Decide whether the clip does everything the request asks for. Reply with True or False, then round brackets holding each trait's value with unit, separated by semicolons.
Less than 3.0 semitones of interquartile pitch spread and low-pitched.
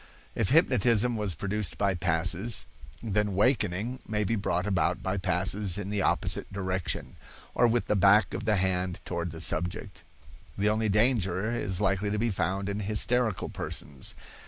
True (2.6 semitones; 100 Hz)